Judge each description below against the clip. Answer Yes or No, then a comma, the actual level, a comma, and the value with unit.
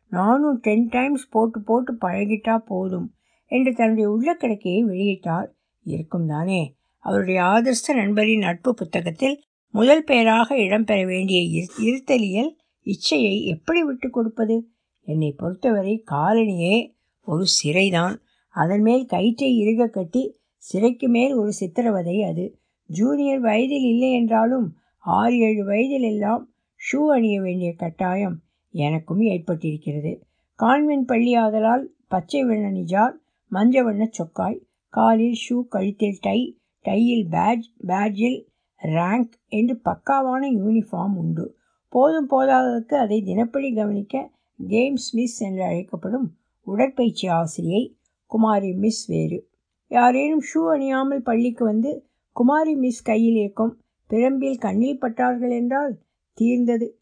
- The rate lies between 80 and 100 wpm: No, average, 110 wpm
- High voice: Yes, high, 225 Hz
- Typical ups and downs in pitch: Yes, average, 4.4 semitones